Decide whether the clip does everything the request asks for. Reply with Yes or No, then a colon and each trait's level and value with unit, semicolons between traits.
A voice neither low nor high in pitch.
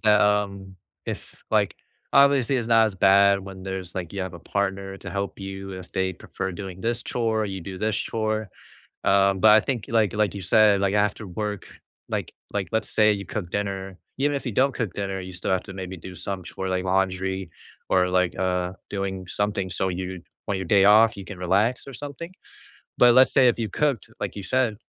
No: low, 100 Hz